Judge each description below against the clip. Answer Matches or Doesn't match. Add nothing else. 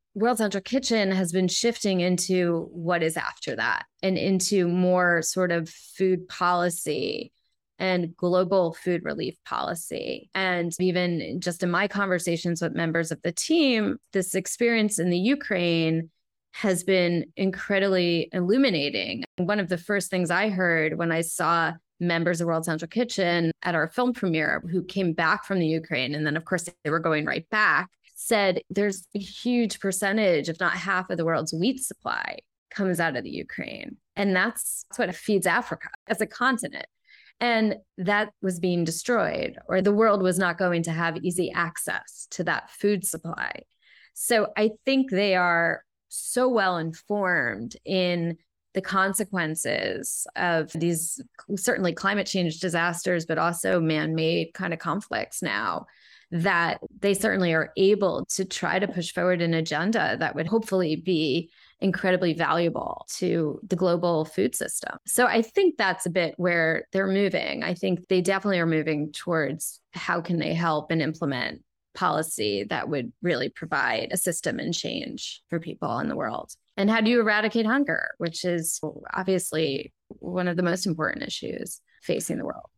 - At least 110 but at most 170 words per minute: Matches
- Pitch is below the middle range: Doesn't match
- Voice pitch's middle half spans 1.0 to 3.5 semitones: Matches